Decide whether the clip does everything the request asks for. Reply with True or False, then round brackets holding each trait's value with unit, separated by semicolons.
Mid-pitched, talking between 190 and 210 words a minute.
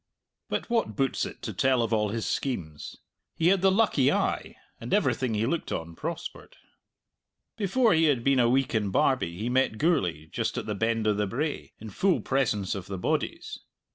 False (125 Hz; 195 wpm)